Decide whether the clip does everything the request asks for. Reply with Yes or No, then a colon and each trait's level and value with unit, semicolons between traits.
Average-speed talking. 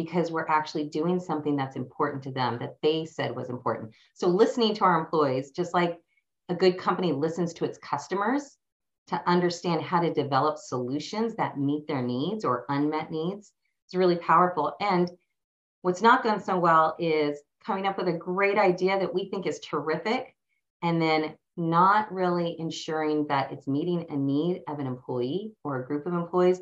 Yes: average, 180 wpm